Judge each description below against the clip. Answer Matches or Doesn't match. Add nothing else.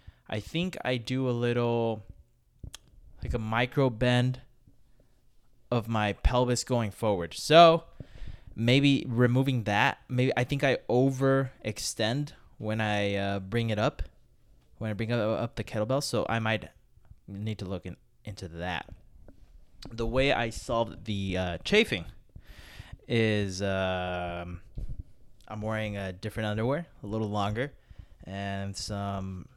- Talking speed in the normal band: Doesn't match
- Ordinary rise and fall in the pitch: Matches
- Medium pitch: Doesn't match